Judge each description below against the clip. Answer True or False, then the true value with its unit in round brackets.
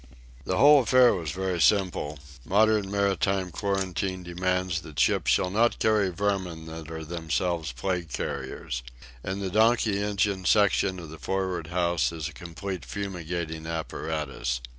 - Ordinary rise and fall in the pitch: True (3.4 semitones)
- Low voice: True (90 Hz)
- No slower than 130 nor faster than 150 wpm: True (140 wpm)